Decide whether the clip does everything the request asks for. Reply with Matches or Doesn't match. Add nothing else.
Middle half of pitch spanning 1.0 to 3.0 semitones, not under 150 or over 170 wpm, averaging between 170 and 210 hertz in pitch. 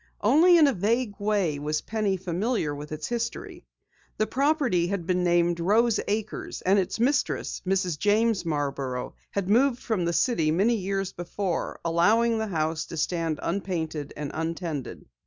Doesn't match